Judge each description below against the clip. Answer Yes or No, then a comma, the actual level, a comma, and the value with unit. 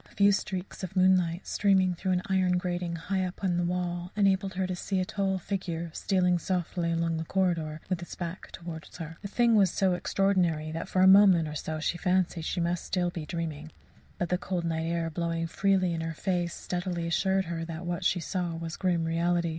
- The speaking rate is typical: No, fast, 215 wpm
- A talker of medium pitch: Yes, medium, 175 Hz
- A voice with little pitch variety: Yes, narrow, 2.0 semitones